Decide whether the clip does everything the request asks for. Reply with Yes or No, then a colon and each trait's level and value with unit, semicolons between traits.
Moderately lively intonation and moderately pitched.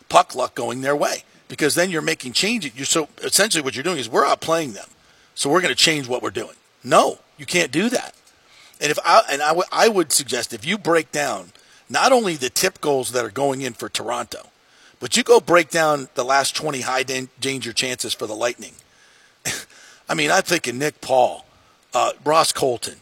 Yes: average, 4.3 semitones; medium, 145 Hz